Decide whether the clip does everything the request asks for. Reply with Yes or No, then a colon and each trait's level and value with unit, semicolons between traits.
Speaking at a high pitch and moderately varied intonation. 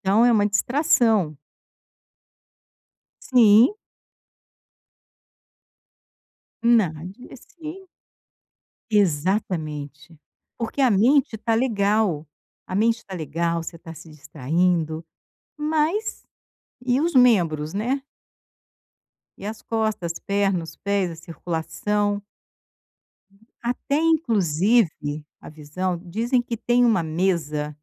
No: high, 200 Hz; wide, 6.3 semitones